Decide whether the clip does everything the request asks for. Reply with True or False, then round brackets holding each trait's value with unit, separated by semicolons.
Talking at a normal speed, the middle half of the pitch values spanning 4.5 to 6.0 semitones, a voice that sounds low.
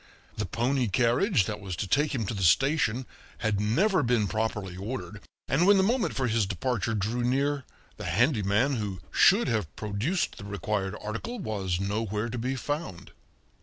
True (170 wpm; 4.9 semitones; 115 Hz)